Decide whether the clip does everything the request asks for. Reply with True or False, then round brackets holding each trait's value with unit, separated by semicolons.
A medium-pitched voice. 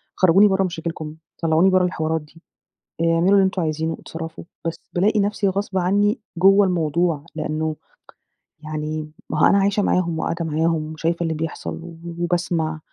True (165 Hz)